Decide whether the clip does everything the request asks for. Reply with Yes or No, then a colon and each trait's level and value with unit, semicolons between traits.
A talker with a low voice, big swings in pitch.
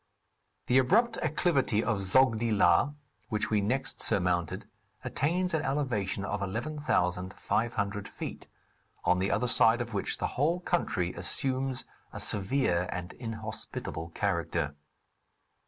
Yes: low, 110 Hz; wide, 6.0 semitones